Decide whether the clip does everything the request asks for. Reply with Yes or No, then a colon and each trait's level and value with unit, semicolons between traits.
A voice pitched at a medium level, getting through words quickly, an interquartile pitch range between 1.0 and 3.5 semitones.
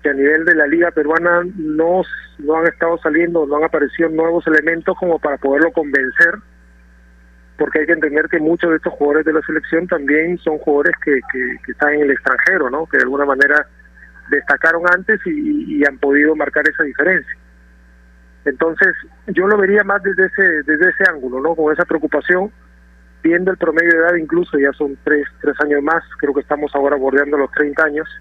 Yes: medium, 155 Hz; fast, 195 wpm; average, 2.7 semitones